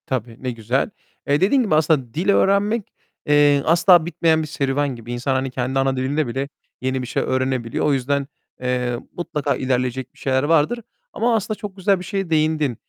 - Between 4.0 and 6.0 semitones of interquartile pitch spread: Yes, average, 4.4 semitones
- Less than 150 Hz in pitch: Yes, medium, 140 Hz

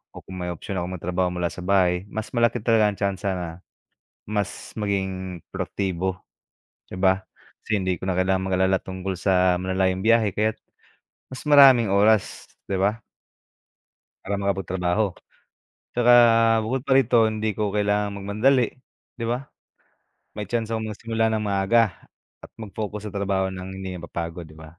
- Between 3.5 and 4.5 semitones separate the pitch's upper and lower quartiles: No, average, 2.9 semitones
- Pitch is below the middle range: Yes, low, 100 Hz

